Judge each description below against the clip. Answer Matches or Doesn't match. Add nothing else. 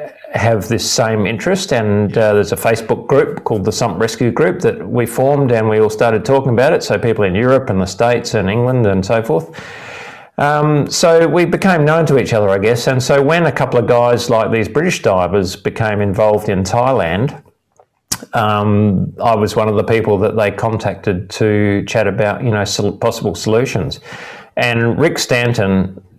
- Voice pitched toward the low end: Matches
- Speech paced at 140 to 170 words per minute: Doesn't match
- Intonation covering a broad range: Doesn't match